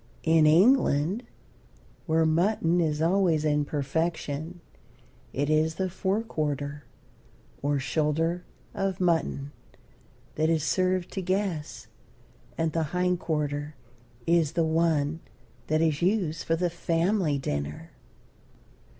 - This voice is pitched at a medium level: Yes, medium, 160 Hz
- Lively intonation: No, average, 3.0 semitones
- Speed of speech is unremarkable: No, slow, 115 wpm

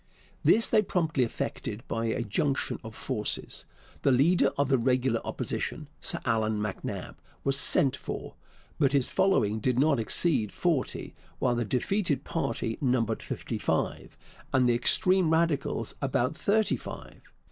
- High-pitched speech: No, low, 130 Hz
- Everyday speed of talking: Yes, average, 145 wpm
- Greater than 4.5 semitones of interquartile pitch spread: Yes, wide, 5.4 semitones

